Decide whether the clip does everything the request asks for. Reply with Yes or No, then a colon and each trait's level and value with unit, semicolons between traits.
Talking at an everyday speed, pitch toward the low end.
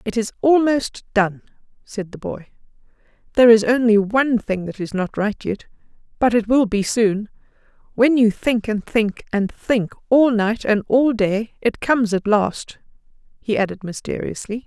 No: average, 170 wpm; high, 220 Hz